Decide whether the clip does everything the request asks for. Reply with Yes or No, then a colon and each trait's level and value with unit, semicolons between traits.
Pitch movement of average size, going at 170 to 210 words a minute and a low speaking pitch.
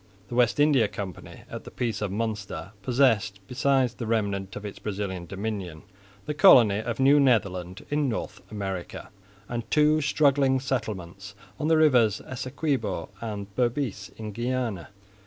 No: average, 5.0 semitones; average, 145 wpm; low, 115 Hz